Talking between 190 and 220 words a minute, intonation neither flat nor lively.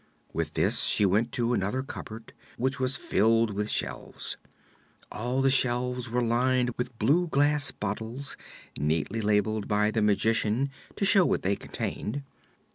No: average, 145 wpm; average, 3.5 semitones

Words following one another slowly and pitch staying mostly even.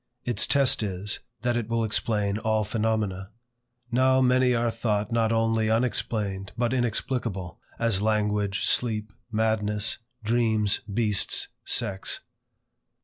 Yes: slow, 115 wpm; narrow, 2.2 semitones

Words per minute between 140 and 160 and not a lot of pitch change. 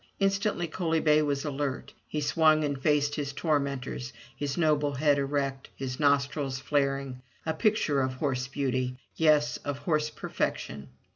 Yes: average, 150 wpm; narrow, 2.0 semitones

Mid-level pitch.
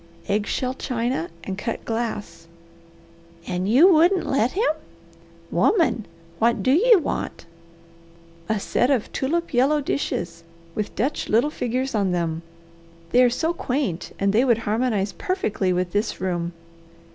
No: high, 235 Hz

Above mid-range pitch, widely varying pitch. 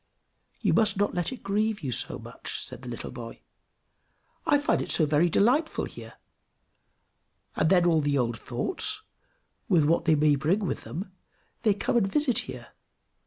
No: medium, 175 Hz; wide, 6.4 semitones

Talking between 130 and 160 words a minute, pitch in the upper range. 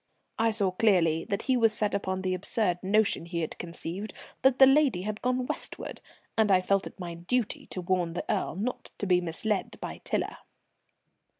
No: average, 190 wpm; high, 195 Hz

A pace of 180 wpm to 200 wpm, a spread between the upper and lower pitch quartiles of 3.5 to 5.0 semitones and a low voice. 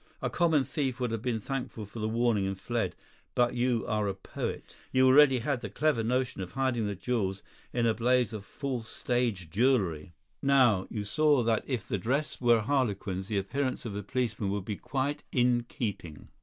Yes: average, 195 wpm; average, 4.0 semitones; low, 120 Hz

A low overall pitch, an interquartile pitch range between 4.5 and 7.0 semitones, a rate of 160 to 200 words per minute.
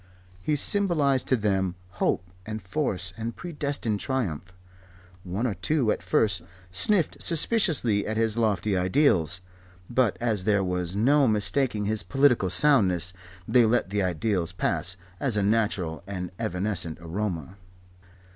No: low, 105 Hz; wide, 5.6 semitones; slow, 135 wpm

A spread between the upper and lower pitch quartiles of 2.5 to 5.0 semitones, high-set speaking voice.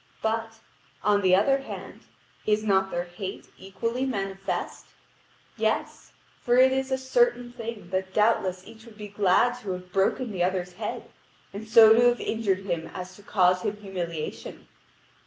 Yes: average, 3.6 semitones; high, 205 Hz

